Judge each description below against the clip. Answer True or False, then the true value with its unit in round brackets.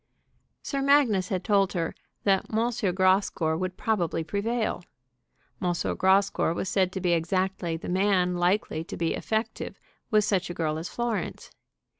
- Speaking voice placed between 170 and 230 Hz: True (190 Hz)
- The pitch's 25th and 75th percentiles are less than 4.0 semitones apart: True (3.1 semitones)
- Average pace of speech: True (150 wpm)